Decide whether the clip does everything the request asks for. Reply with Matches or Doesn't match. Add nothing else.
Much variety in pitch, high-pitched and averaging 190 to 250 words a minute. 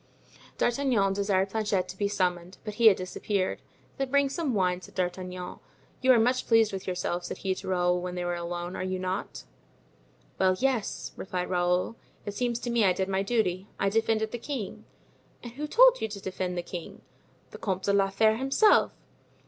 Doesn't match